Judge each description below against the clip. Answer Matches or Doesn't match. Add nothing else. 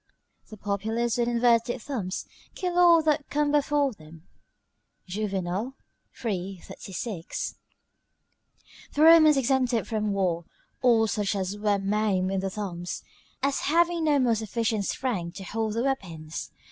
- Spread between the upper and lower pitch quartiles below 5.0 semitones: Doesn't match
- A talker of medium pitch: Doesn't match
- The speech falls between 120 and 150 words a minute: Matches